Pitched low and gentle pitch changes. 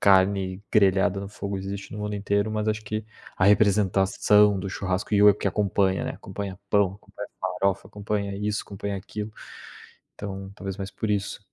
Yes: low, 100 Hz; narrow, 1.2 semitones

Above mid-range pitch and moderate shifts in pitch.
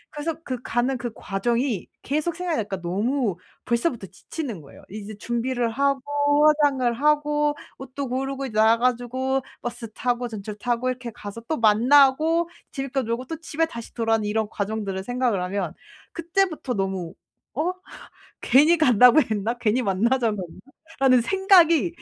Yes: very high, 250 Hz; average, 4.7 semitones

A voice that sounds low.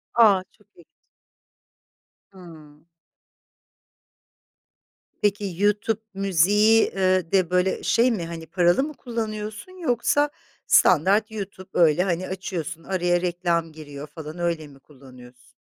No: medium, 185 Hz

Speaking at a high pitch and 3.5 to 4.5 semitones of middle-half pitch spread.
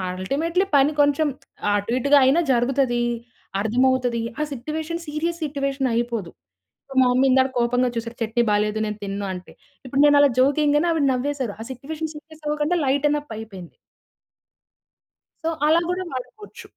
Yes: very high, 270 Hz; average, 4.0 semitones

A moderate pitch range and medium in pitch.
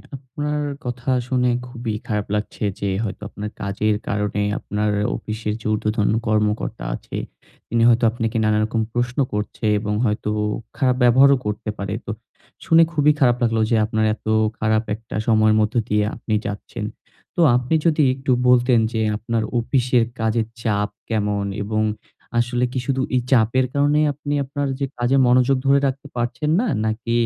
No: average, 3.1 semitones; low, 115 Hz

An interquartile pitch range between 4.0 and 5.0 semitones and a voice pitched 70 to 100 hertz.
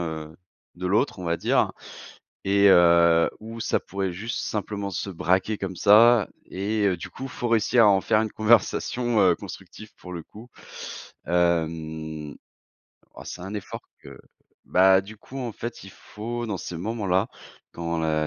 Yes: average, 4.3 semitones; very low, 95 Hz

